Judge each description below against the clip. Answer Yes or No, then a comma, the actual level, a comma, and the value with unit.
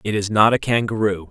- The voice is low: Yes, low, 105 Hz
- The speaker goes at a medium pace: No, fast, 230 wpm